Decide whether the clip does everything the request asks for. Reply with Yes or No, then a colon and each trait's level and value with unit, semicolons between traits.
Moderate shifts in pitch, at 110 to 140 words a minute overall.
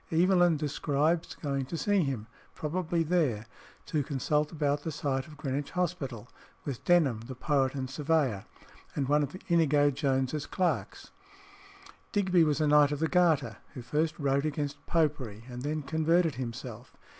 No: average, 3.2 semitones; average, 155 wpm